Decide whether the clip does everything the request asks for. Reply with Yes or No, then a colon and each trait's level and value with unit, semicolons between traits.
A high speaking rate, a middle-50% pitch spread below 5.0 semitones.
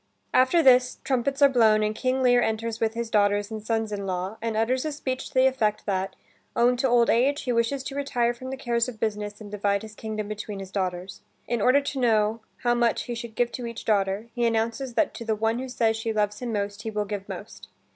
Yes: fast, 240 wpm; average, 3.0 semitones